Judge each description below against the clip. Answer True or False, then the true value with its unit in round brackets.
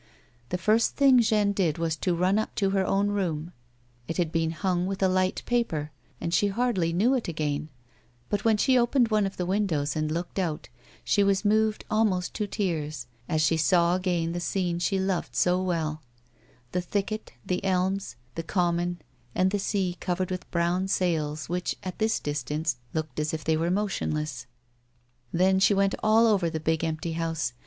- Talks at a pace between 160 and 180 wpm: False (190 wpm)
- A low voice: False (180 Hz)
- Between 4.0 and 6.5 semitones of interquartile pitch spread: False (3.5 semitones)